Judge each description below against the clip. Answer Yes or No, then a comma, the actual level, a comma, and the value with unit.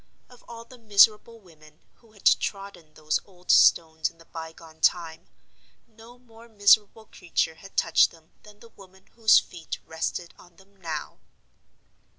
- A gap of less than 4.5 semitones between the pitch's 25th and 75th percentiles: No, average, 5.1 semitones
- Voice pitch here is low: No, high, 190 Hz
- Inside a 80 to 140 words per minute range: No, average, 155 wpm